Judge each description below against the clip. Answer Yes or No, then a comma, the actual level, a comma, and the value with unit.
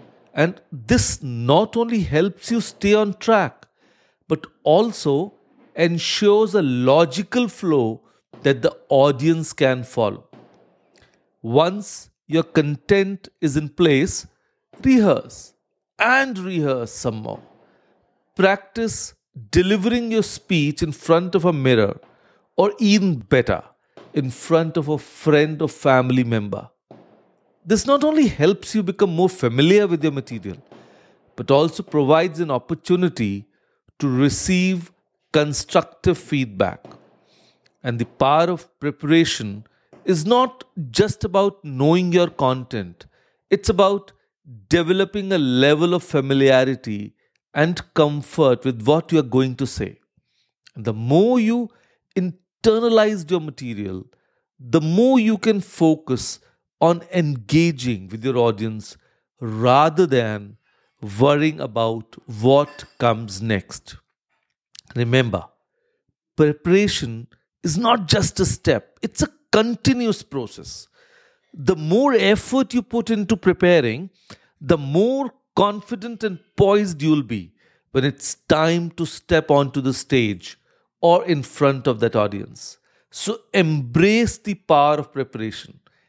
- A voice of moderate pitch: Yes, medium, 160 Hz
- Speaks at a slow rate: Yes, slow, 115 wpm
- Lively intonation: Yes, wide, 7.0 semitones